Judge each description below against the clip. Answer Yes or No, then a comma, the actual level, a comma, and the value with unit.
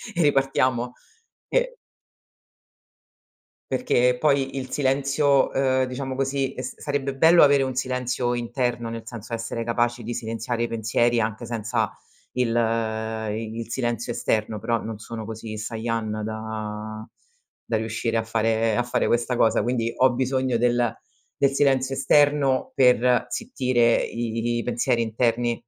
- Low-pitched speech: Yes, low, 120 Hz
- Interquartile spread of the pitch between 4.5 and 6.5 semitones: No, narrow, 2.5 semitones